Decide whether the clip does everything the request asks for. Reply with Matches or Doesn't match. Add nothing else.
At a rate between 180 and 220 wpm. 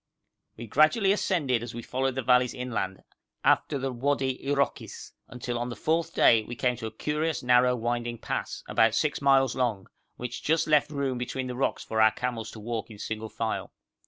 Matches